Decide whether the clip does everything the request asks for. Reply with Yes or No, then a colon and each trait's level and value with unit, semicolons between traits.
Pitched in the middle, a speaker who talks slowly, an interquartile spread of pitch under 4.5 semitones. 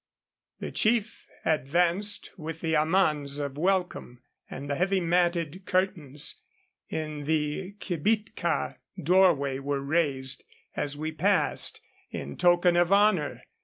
Yes: medium, 165 Hz; slow, 110 wpm; average, 4.1 semitones